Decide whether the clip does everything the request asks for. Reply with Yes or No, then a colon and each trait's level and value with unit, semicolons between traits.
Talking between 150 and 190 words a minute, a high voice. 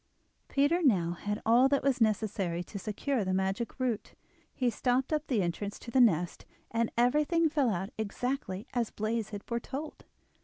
Yes: average, 165 wpm; high, 230 Hz